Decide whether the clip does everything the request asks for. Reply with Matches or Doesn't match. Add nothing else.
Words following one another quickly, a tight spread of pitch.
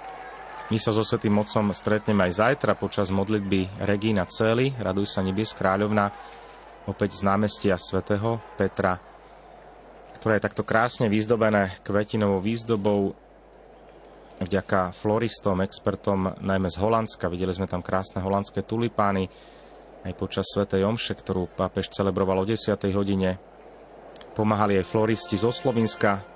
Doesn't match